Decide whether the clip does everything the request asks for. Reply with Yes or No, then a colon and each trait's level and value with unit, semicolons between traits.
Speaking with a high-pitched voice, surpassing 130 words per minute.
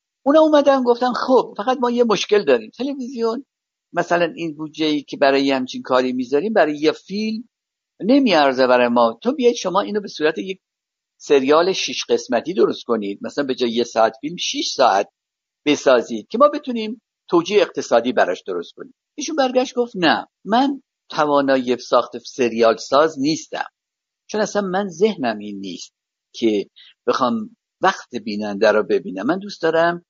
Yes: high, 195 Hz; fast, 155 wpm